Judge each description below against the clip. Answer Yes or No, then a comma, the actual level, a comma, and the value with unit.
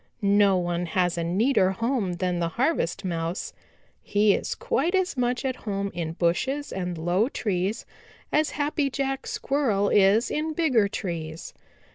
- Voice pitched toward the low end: No, high, 200 Hz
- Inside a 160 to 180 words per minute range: No, average, 150 wpm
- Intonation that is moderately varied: No, wide, 7.3 semitones